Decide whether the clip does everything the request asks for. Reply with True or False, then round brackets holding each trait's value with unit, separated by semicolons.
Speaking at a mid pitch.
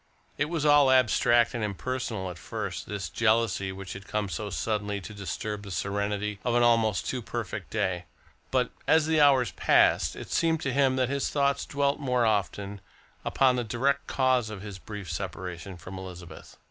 False (110 Hz)